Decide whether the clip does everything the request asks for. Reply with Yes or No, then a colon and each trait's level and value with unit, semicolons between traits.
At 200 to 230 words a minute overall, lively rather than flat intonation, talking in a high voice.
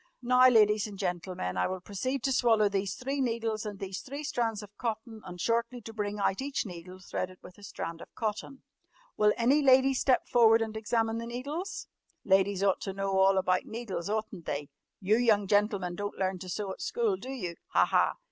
No: fast, 205 wpm; average, 3.8 semitones; high, 210 Hz